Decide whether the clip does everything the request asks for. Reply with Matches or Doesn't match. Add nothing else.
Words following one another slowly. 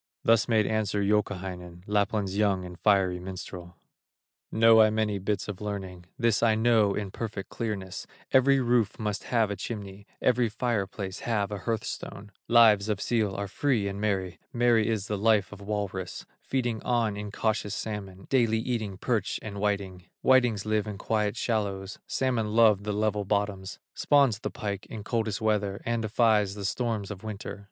Doesn't match